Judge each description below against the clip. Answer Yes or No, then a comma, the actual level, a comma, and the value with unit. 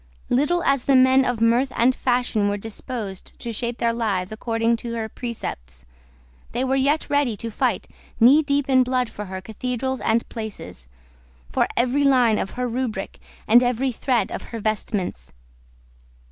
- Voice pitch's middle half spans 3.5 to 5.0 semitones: No, average, 3.0 semitones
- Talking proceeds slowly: No, average, 165 wpm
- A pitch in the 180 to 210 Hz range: No, high, 235 Hz